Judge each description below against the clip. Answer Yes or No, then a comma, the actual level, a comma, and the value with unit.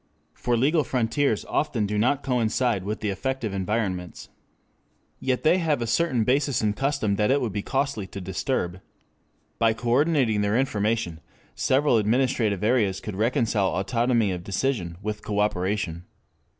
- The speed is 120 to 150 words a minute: Yes, average, 145 wpm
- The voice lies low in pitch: Yes, low, 110 Hz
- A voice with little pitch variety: No, average, 4.4 semitones